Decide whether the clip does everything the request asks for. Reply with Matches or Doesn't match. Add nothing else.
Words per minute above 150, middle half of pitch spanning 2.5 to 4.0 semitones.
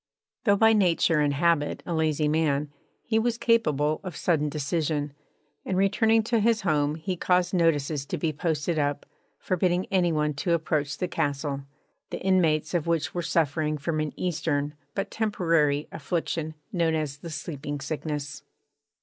Matches